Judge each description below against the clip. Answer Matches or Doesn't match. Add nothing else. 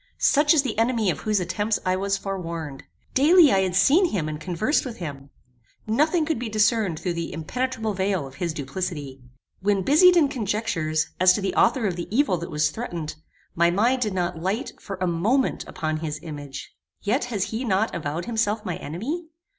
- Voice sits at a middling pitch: Doesn't match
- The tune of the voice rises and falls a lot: Matches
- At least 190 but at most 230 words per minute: Matches